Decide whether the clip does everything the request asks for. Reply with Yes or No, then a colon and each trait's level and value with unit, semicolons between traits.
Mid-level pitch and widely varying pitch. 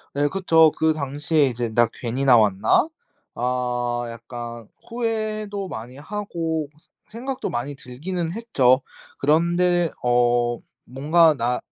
Yes: medium, 145 Hz; wide, 6.2 semitones